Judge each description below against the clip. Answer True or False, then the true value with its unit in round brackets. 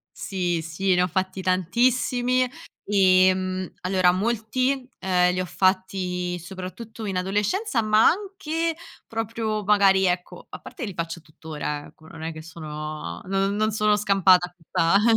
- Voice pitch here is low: False (190 Hz)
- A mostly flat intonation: False (3.3 semitones)